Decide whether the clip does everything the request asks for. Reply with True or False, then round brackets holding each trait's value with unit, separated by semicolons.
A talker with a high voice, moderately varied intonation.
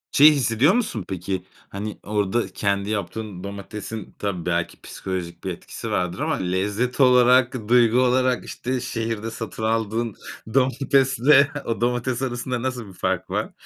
False (115 Hz; 4.1 semitones)